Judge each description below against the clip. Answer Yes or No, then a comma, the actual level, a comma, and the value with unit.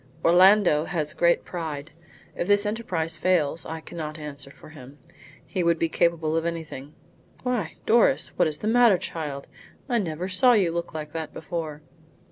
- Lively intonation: No, average, 3.2 semitones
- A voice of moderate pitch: Yes, medium, 165 Hz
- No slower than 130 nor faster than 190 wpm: Yes, average, 165 wpm